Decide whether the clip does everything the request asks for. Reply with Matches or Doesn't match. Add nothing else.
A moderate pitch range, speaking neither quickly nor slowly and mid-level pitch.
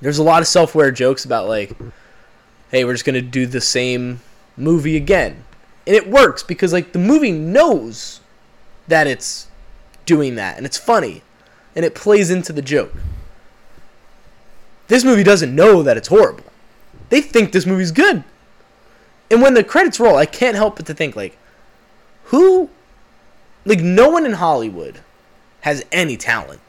Doesn't match